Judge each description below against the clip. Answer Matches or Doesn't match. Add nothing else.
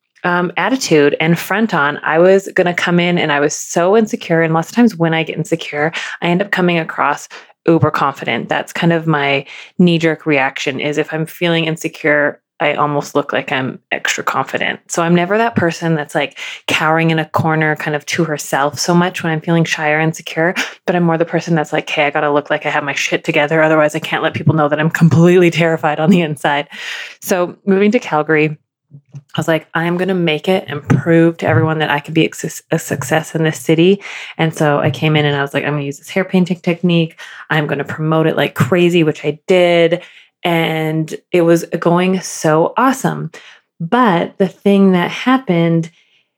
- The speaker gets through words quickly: Matches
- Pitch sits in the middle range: Matches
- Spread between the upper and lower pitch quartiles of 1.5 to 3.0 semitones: Matches